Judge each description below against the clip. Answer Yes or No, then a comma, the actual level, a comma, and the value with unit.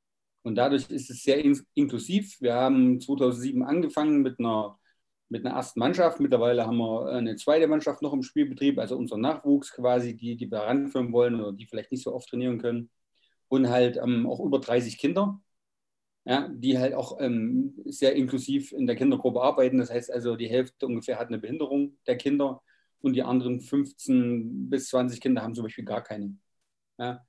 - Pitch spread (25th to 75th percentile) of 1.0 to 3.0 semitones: Yes, average, 2.7 semitones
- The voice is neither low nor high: No, low, 130 Hz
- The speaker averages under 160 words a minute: No, average, 185 wpm